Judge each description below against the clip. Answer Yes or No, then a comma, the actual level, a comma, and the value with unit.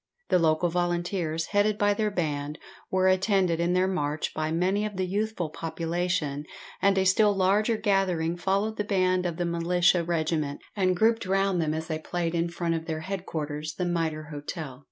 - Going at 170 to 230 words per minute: Yes, average, 180 wpm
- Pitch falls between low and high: Yes, medium, 175 Hz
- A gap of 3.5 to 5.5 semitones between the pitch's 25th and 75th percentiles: No, average, 3.1 semitones